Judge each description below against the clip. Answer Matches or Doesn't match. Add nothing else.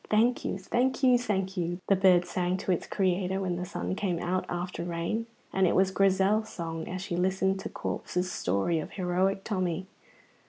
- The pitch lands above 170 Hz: Matches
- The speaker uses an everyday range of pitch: Doesn't match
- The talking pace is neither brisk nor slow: Matches